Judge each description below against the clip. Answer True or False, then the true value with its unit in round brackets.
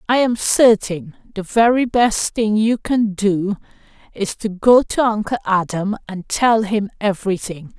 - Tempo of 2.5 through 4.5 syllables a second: True (4.1 syllables/s)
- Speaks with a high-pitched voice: True (210 Hz)